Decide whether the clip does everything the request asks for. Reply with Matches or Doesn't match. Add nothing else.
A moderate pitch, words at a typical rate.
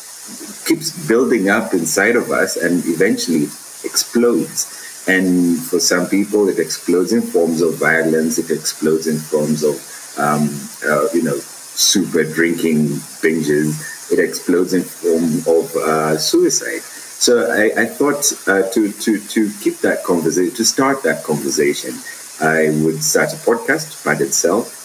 Doesn't match